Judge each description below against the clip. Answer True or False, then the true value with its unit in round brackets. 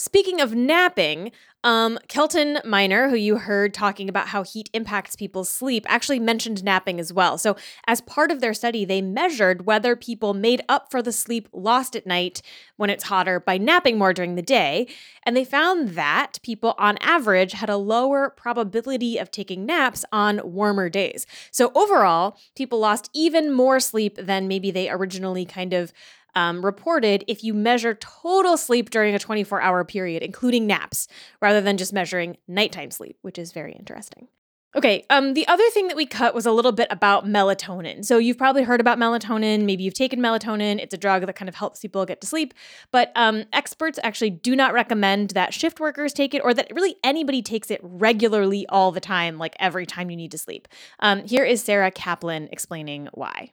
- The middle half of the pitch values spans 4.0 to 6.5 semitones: True (4.4 semitones)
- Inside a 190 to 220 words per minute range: True (195 wpm)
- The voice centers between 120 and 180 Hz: False (215 Hz)